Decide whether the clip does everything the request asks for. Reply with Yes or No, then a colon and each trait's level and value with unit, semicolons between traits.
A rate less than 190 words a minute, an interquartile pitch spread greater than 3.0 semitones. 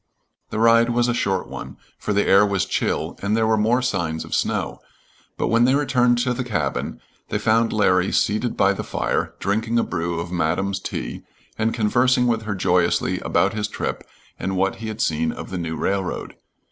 No: average, 195 wpm; average, 3.5 semitones